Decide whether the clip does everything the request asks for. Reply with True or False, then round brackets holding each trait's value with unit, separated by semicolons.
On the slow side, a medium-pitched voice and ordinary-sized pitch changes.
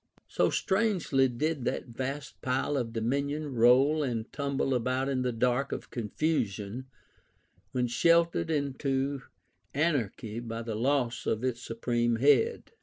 False (130 wpm; 130 Hz; 3.3 semitones)